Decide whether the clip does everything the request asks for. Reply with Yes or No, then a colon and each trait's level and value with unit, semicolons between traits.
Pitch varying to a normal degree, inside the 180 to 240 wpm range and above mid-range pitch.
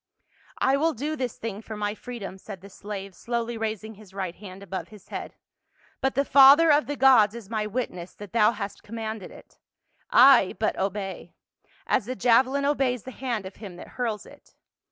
Yes: average, 4.4 semitones; average, 200 wpm; high, 220 Hz